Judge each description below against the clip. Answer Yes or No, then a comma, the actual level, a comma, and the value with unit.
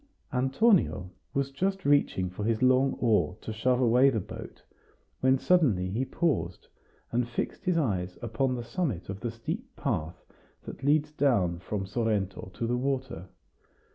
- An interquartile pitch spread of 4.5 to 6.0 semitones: Yes, wide, 5.5 semitones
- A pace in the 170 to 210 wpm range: No, average, 155 wpm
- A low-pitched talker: Yes, low, 120 Hz